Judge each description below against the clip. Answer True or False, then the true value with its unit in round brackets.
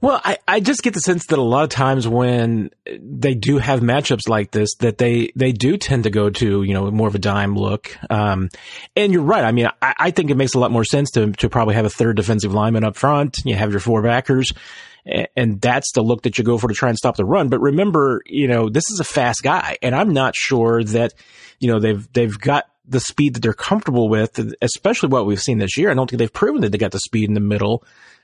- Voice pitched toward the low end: True (120 Hz)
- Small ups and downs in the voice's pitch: False (3.7 semitones)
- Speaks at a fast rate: True (265 wpm)